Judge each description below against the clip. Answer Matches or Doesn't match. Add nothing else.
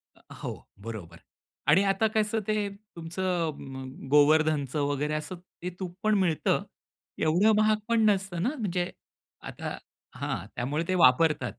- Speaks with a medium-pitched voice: Matches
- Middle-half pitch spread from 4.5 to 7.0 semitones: Matches